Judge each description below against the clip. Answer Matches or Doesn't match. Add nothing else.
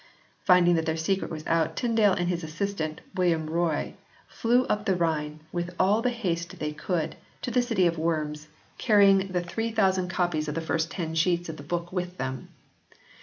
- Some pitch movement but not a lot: Matches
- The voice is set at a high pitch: Doesn't match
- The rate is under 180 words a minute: Doesn't match